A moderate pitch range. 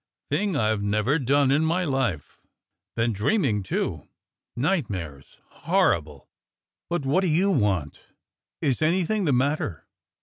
No: wide, 7.8 semitones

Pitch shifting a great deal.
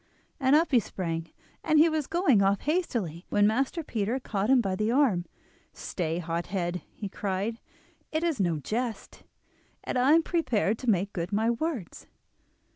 Yes: wide, 6.3 semitones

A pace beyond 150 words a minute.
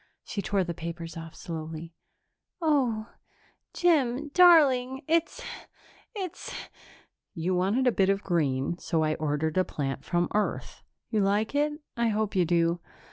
No: average, 145 wpm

